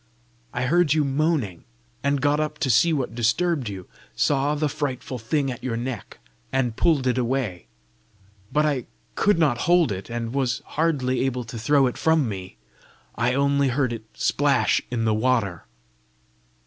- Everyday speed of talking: Yes, average, 165 wpm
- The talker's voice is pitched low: Yes, low, 130 Hz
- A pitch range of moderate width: Yes, average, 3.9 semitones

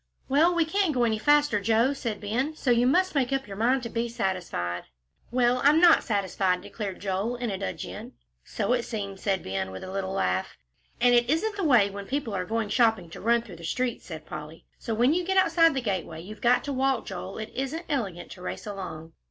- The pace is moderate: No, fast, 225 wpm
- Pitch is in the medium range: No, high, 230 Hz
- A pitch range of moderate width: No, wide, 5.7 semitones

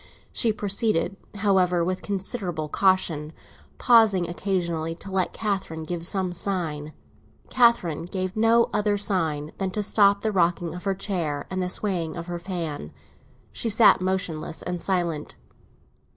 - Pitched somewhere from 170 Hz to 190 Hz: Yes, medium, 185 Hz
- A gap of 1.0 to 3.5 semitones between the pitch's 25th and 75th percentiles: Yes, average, 3.2 semitones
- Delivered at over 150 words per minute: No, average, 140 wpm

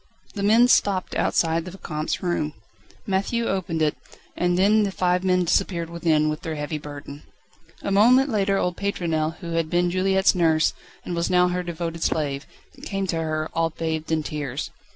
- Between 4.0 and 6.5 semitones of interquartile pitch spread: No, average, 3.4 semitones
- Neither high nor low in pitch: Yes, medium, 175 Hz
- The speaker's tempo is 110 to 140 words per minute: No, average, 175 wpm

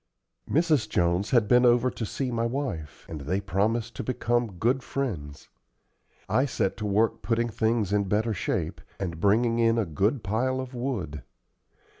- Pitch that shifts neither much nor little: Yes, average, 3.9 semitones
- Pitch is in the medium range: No, low, 115 Hz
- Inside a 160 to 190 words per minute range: Yes, average, 165 wpm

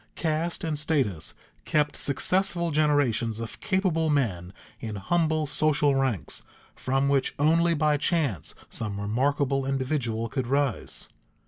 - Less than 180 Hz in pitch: Yes, medium, 140 Hz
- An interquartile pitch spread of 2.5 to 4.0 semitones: No, average, 4.8 semitones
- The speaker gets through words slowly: Yes, slow, 120 wpm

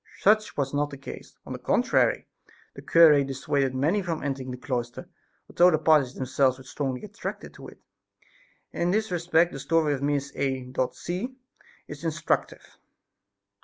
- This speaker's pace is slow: No, average, 160 wpm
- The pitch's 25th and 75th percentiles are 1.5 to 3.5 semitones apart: No, average, 4.4 semitones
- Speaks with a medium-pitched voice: Yes, medium, 145 Hz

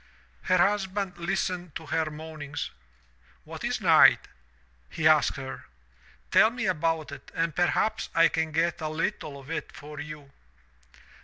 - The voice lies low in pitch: No, medium, 160 Hz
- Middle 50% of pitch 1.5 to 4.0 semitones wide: Yes, average, 2.8 semitones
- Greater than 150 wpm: No, average, 145 wpm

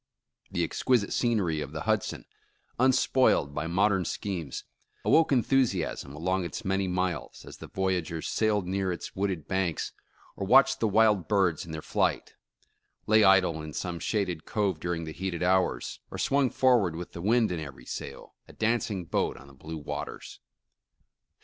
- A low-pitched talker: Yes, very low, 95 Hz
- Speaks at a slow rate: No, average, 160 wpm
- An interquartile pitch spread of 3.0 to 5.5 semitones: Yes, average, 4.4 semitones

